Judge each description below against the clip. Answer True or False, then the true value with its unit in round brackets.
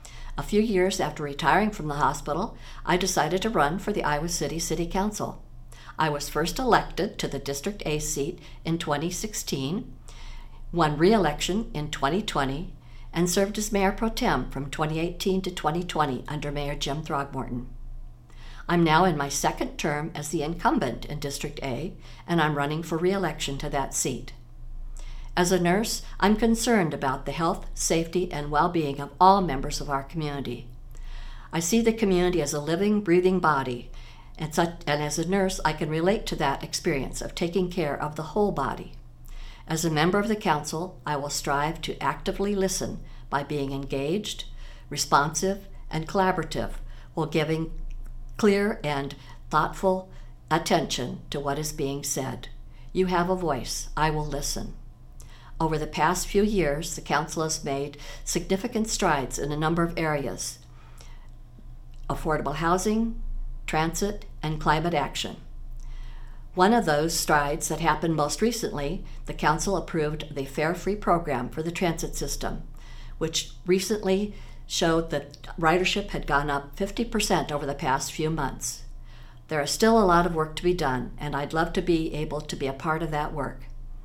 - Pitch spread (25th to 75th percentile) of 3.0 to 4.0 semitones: False (4.5 semitones)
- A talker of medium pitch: True (155 Hz)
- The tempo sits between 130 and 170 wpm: True (160 wpm)